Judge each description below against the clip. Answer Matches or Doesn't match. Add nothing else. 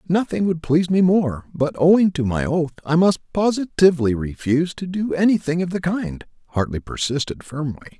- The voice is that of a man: Matches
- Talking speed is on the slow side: Doesn't match